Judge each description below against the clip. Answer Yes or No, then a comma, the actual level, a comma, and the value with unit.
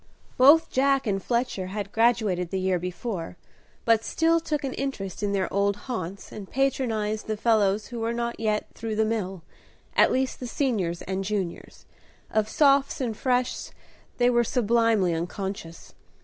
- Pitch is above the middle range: Yes, high, 220 Hz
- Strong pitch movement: No, average, 4.2 semitones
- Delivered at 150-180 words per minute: Yes, average, 160 wpm